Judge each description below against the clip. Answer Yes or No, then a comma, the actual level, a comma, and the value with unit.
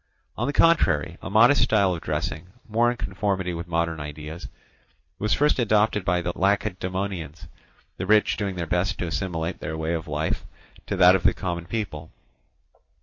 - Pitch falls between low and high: No, very low, 90 Hz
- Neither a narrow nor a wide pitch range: Yes, average, 3.9 semitones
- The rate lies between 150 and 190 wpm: Yes, average, 170 wpm